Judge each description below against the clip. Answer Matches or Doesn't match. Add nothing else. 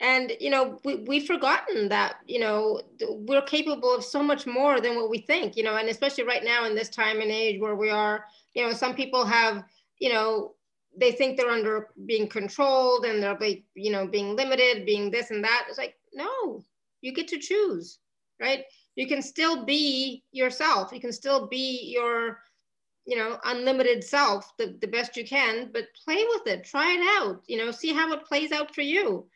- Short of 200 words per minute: Doesn't match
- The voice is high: Matches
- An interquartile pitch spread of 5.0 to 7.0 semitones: Doesn't match